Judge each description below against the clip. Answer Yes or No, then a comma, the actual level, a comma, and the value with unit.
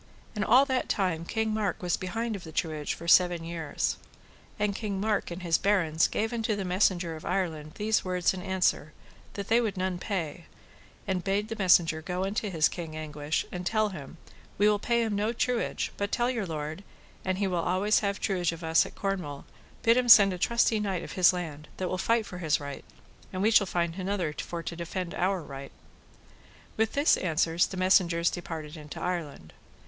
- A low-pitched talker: No, medium, 185 Hz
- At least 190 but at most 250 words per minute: Yes, average, 200 wpm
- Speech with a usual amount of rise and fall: Yes, average, 3.8 semitones